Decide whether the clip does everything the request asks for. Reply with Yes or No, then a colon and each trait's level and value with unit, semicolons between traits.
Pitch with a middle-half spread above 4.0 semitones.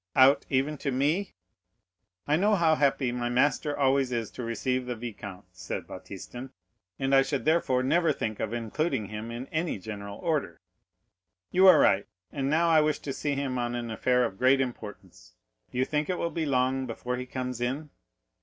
No: average, 3.7 semitones